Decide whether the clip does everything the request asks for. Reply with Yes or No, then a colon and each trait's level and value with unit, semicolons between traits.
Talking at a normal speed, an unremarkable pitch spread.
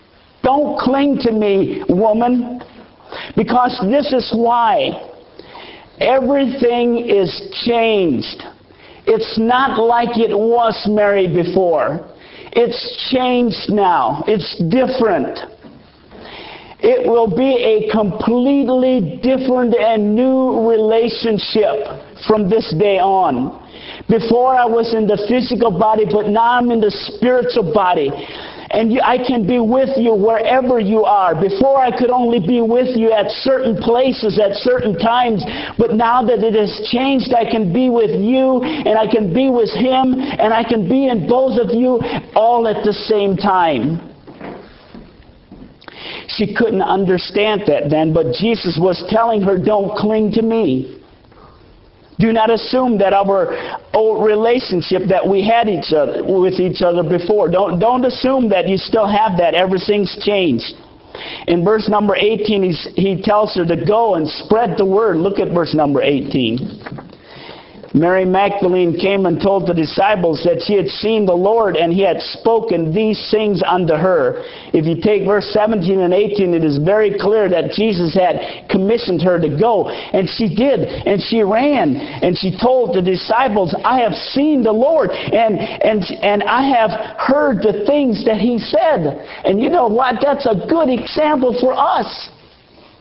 Yes: average, 155 wpm; average, 3.9 semitones